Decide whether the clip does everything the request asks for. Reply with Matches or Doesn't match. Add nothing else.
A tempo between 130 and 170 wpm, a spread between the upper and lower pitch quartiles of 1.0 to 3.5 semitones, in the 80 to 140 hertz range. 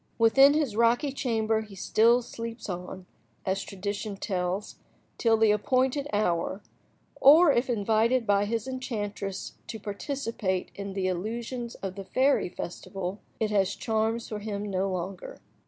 Doesn't match